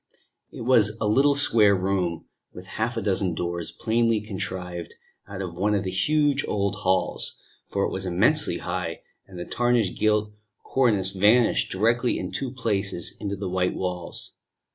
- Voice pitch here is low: Yes, low, 100 Hz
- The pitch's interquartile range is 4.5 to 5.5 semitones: No, average, 3.8 semitones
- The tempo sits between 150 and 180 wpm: Yes, average, 165 wpm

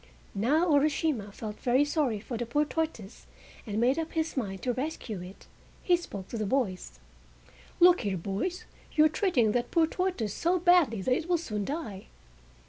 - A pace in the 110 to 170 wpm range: No, average, 180 wpm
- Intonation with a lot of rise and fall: Yes, wide, 7.4 semitones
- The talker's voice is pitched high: Yes, very high, 255 Hz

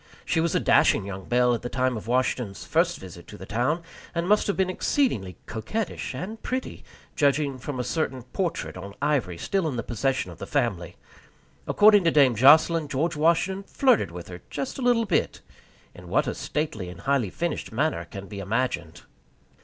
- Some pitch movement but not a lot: No, wide, 7.7 semitones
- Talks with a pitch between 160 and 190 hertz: No, low, 135 Hz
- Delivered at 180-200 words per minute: Yes, average, 190 wpm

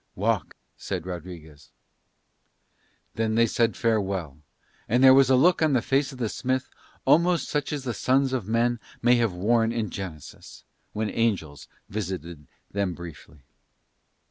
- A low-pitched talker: Yes, low, 110 Hz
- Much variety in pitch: Yes, wide, 6.1 semitones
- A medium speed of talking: Yes, average, 145 wpm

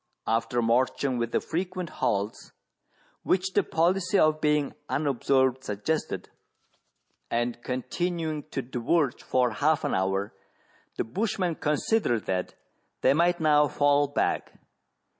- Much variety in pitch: Yes, wide, 5.7 semitones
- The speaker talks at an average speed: No, slow, 120 wpm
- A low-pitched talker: No, medium, 145 Hz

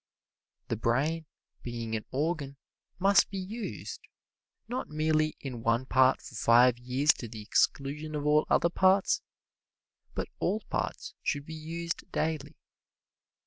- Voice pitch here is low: No, medium, 150 Hz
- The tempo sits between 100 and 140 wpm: Yes, slow, 135 wpm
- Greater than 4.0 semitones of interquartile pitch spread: Yes, average, 4.7 semitones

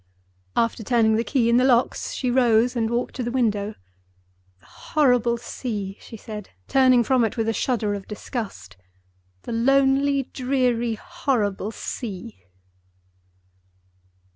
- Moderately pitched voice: No, high, 235 Hz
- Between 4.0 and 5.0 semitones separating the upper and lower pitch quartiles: No, average, 3.3 semitones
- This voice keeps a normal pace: No, slow, 130 wpm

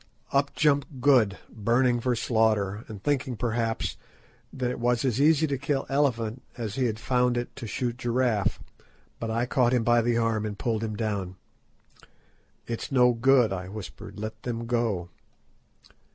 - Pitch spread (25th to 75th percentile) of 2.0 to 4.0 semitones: Yes, narrow, 2.6 semitones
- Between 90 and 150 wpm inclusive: No, average, 165 wpm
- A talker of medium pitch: No, low, 120 Hz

